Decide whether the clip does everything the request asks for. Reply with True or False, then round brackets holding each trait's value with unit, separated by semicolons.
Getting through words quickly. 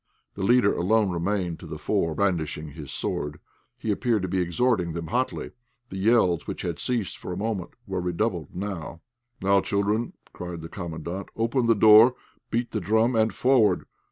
False (175 wpm)